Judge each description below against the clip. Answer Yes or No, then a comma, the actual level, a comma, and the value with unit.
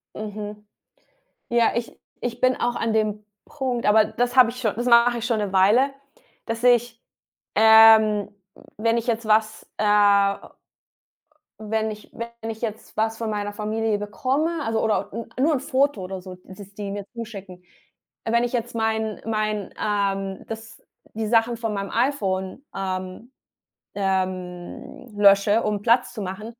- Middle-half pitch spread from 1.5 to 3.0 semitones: Yes, narrow, 2.4 semitones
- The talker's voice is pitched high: Yes, high, 220 Hz